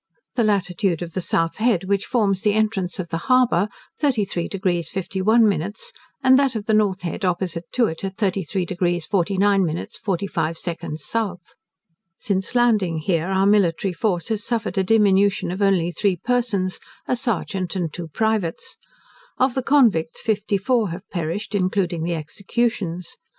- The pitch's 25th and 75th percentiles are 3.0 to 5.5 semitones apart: Yes, average, 3.7 semitones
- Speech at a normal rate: Yes, average, 160 wpm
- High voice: Yes, high, 195 Hz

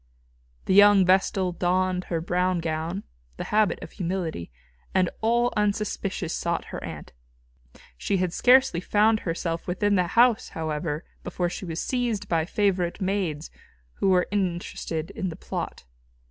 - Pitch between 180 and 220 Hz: Yes, medium, 185 Hz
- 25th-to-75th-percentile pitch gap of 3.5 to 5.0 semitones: No, average, 3.1 semitones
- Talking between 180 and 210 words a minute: No, average, 145 wpm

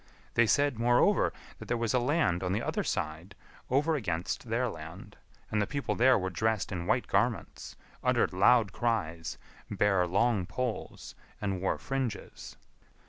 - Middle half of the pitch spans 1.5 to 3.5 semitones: No, average, 4.7 semitones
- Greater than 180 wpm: No, average, 155 wpm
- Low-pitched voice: Yes, low, 110 Hz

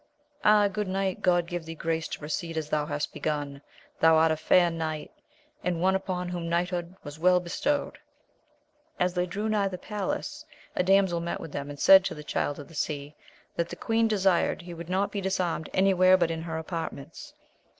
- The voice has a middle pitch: Yes, medium, 175 Hz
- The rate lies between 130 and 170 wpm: No, average, 200 wpm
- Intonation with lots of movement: No, average, 2.9 semitones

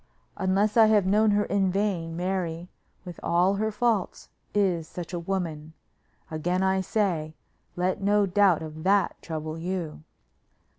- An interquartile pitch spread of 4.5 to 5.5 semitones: No, average, 3.3 semitones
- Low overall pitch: No, medium, 185 Hz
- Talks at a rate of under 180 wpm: Yes, average, 145 wpm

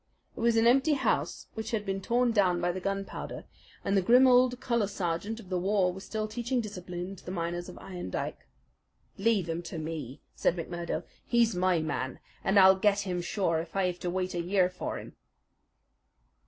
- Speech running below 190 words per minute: No, average, 200 wpm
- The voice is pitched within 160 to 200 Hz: Yes, high, 190 Hz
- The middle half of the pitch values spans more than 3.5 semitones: Yes, average, 3.9 semitones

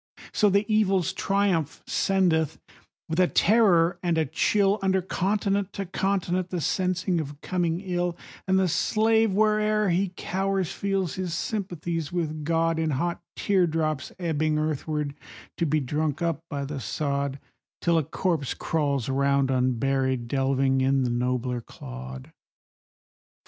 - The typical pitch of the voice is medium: Yes, medium, 165 Hz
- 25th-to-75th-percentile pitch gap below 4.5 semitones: No, average, 5.2 semitones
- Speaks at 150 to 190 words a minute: No, average, 140 wpm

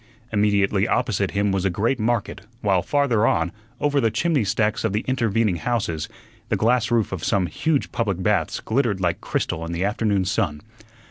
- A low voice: Yes, low, 105 Hz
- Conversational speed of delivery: Yes, average, 180 wpm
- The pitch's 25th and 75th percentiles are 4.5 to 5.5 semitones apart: No, average, 3.5 semitones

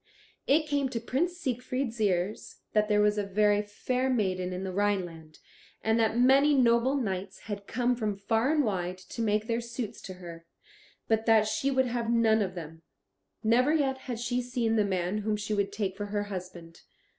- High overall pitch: Yes, high, 215 Hz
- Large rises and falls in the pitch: No, average, 3.9 semitones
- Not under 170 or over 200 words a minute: Yes, average, 190 wpm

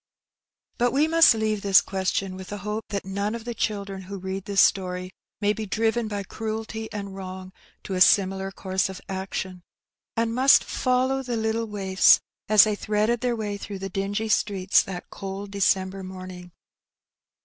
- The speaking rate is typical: Yes, average, 170 wpm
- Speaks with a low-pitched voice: No, high, 200 Hz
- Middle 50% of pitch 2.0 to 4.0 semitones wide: Yes, narrow, 2.5 semitones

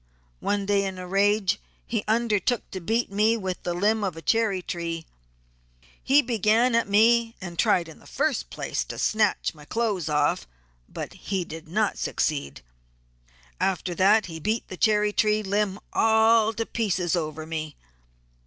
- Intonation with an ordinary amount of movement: Yes, average, 4.1 semitones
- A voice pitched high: Yes, high, 200 Hz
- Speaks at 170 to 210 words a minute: No, average, 160 wpm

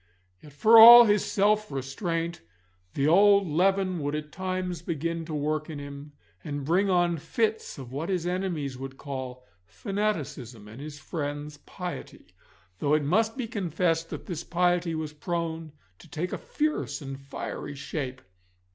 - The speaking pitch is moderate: Yes, medium, 165 Hz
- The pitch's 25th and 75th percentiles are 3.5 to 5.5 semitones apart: Yes, average, 4.4 semitones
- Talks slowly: No, average, 155 wpm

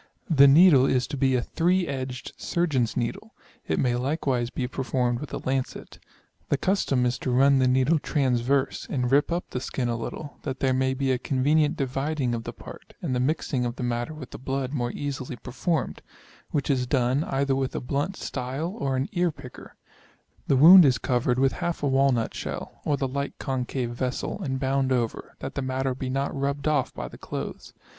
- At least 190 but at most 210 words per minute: Yes, fast, 205 wpm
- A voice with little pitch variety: Yes, narrow, 2.1 semitones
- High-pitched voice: No, low, 135 Hz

